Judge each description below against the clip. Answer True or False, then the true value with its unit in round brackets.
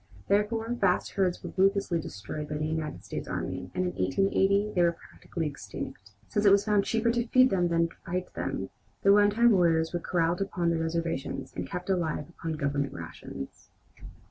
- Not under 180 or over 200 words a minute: True (185 wpm)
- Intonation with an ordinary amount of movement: True (4.0 semitones)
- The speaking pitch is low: False (175 Hz)